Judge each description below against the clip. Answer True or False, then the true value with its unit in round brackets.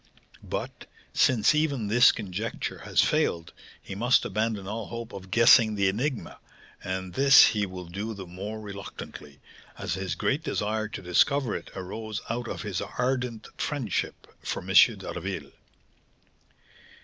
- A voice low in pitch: True (110 Hz)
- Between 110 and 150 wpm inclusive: True (140 wpm)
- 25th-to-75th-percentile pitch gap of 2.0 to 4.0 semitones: True (3.7 semitones)